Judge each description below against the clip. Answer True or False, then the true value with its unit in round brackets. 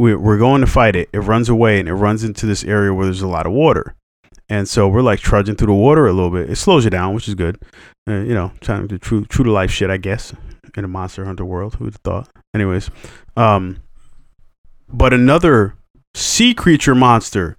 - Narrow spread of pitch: False (3.2 semitones)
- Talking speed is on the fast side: True (220 wpm)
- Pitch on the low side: True (105 Hz)